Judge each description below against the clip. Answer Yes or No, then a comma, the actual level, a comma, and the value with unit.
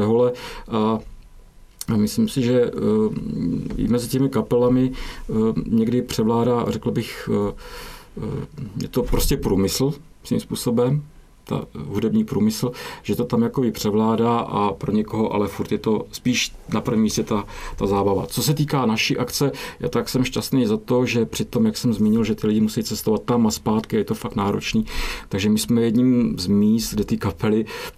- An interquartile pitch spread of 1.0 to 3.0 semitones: Yes, average, 2.7 semitones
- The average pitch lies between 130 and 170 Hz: No, low, 115 Hz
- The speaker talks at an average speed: Yes, average, 170 wpm